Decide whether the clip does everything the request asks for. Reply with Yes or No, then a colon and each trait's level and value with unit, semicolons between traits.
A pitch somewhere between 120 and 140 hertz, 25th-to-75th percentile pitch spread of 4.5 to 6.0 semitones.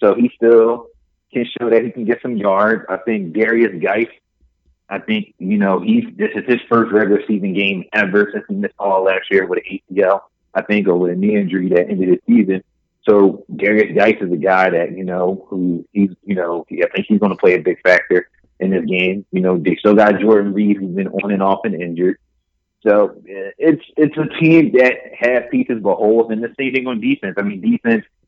No: low, 105 Hz; average, 5.1 semitones